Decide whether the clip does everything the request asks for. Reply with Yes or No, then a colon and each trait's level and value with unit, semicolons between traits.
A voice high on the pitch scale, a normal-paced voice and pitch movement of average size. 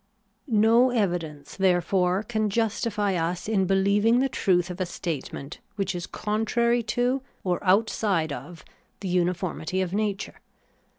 No: high, 195 Hz; slow, 130 wpm; average, 3.5 semitones